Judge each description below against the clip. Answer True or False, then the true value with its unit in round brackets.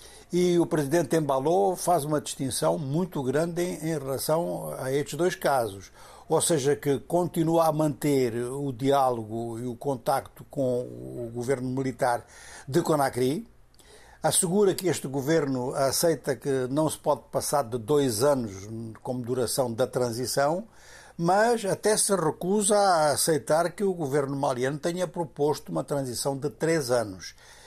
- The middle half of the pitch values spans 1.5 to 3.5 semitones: False (4.3 semitones)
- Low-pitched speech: False (145 Hz)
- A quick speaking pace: False (145 wpm)